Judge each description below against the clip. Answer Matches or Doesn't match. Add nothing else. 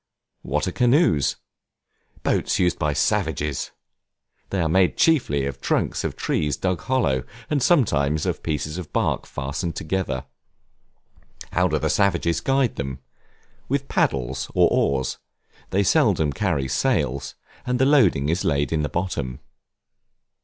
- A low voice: Matches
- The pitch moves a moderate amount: Doesn't match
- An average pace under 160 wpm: Matches